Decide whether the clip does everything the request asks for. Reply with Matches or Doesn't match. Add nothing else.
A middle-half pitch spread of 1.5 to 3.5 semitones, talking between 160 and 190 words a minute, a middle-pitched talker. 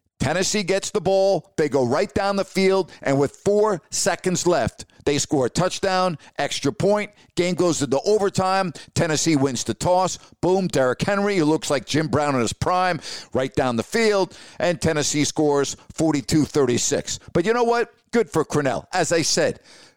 Doesn't match